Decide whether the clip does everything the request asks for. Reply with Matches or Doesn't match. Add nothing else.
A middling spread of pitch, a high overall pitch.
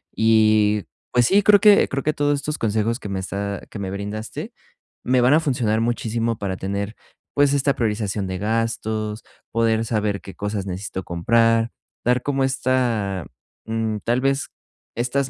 Doesn't match